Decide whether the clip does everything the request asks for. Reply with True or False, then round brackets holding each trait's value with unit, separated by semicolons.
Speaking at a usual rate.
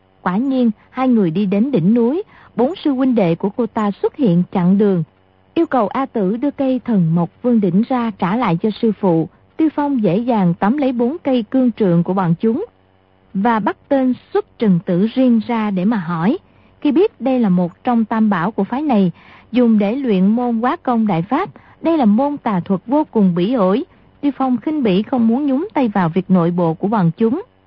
True (220 wpm)